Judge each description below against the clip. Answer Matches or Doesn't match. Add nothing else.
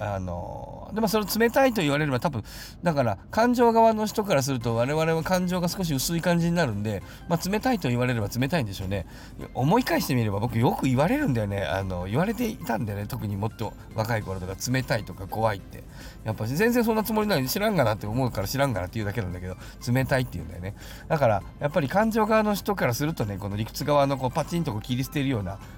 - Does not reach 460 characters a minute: Doesn't match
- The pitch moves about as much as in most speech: Doesn't match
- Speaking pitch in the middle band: Doesn't match